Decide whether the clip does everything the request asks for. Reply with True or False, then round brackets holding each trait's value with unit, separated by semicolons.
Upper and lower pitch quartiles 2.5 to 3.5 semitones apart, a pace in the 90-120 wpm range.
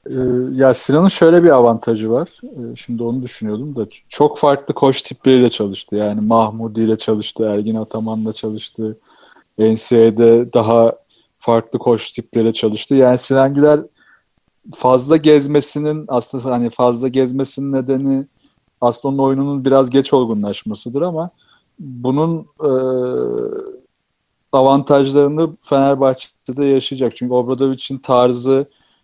True (3.2 semitones; 110 wpm)